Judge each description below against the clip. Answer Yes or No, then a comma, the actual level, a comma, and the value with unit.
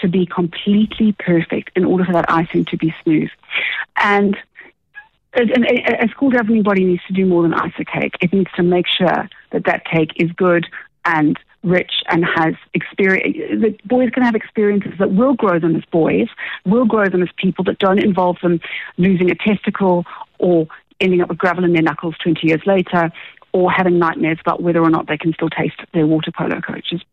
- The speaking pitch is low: No, medium, 180 Hz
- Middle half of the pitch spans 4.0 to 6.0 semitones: No, average, 3.3 semitones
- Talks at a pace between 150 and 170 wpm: No, average, 200 wpm